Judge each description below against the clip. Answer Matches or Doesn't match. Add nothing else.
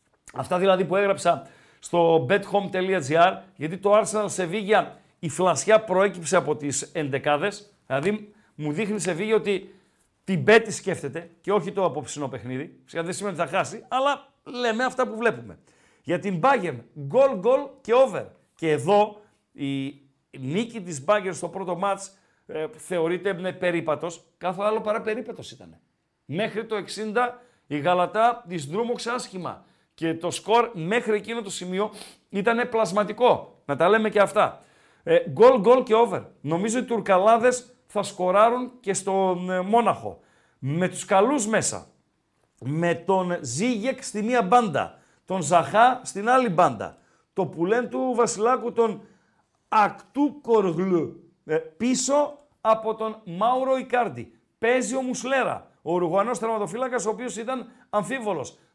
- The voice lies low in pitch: Doesn't match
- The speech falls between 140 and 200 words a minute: Matches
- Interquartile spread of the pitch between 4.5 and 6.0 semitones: Matches